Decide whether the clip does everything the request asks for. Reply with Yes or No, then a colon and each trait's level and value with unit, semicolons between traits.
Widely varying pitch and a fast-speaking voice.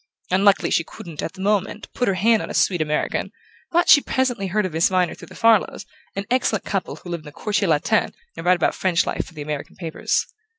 No: average, 4.0 semitones; fast, 230 wpm